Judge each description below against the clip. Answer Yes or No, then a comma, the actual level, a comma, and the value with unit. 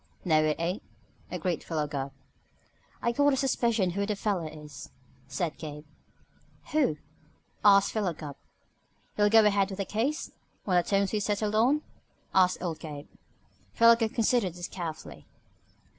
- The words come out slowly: No, average, 150 wpm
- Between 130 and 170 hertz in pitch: No, high, 195 Hz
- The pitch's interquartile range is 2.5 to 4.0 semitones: No, average, 5.2 semitones